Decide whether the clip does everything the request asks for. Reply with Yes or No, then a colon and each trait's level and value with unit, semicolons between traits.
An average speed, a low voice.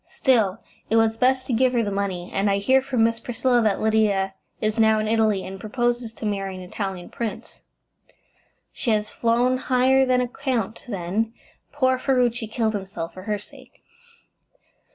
No: average, 175 wpm; high, 225 Hz